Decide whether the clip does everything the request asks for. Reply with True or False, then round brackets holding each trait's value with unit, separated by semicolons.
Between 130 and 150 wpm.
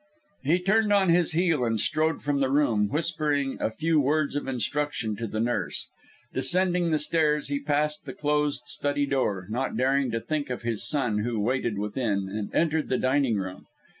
False (185 wpm)